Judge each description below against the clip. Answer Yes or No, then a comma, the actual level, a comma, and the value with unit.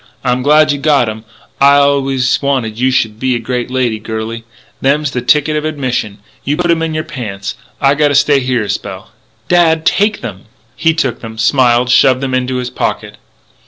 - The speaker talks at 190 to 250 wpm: Yes, average, 200 wpm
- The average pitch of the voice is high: No, low, 130 Hz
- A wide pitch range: No, average, 3.6 semitones